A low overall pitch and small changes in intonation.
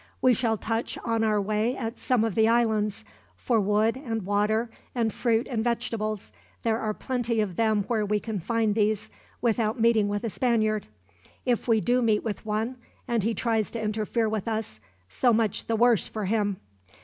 No: high, 220 Hz; narrow, 1.6 semitones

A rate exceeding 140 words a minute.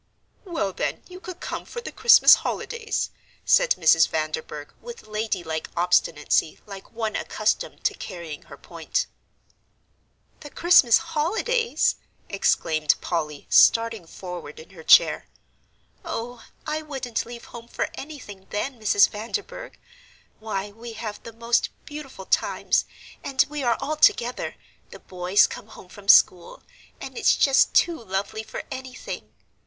No: slow, 135 wpm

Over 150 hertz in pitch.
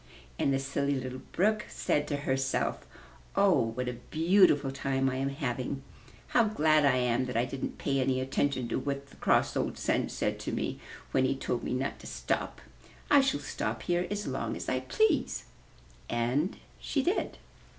No: low, 135 Hz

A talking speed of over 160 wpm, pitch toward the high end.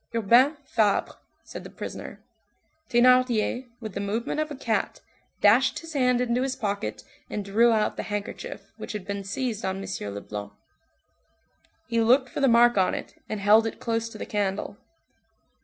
Yes: average, 170 wpm; high, 225 Hz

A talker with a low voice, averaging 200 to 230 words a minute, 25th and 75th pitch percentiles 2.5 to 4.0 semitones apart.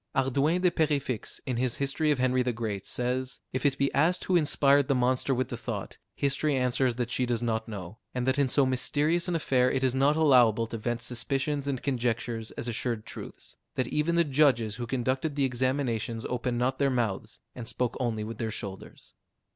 Yes: low, 130 Hz; fast, 205 wpm; average, 2.8 semitones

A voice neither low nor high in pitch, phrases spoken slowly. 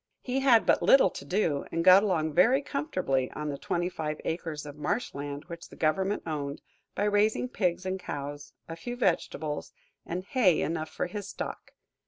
No: medium, 175 Hz; average, 185 wpm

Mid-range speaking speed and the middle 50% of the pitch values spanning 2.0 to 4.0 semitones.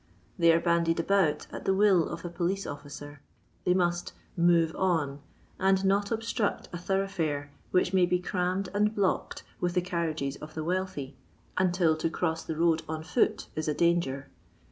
Yes: average, 180 wpm; average, 2.9 semitones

